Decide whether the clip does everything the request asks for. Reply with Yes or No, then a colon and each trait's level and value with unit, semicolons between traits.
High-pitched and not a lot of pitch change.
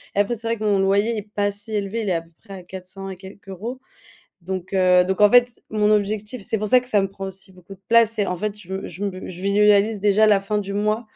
Yes: high, 200 Hz; narrow, 1.8 semitones